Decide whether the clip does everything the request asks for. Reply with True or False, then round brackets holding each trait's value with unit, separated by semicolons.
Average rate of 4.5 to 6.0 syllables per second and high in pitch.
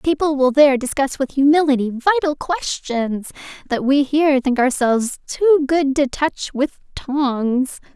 False (4.3 syllables/s; 280 Hz)